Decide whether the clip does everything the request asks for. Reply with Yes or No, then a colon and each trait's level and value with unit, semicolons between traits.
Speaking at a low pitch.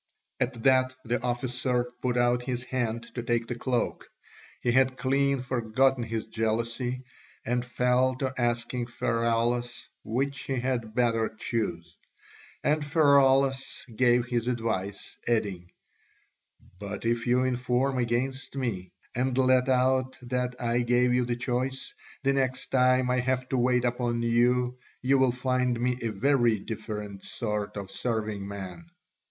Yes: low, 125 Hz